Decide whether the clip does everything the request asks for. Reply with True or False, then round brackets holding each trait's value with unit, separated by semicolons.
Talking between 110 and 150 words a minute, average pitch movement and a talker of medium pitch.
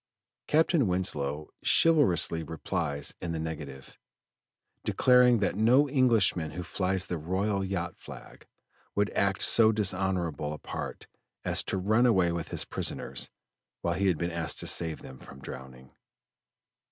False (140 wpm; 4.8 semitones; 90 Hz)